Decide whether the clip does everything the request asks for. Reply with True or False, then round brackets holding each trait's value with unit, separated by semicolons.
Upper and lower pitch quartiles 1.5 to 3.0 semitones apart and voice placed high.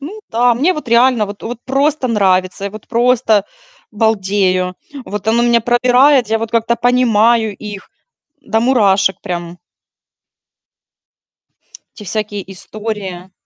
False (3.4 semitones; 220 Hz)